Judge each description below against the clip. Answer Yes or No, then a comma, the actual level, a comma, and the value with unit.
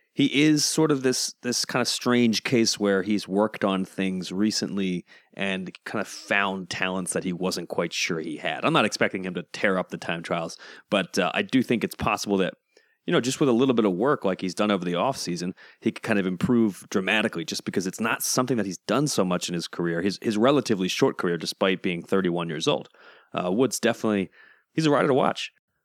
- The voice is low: Yes, low, 100 Hz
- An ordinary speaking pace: No, fast, 230 wpm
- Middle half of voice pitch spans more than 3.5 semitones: Yes, average, 4.1 semitones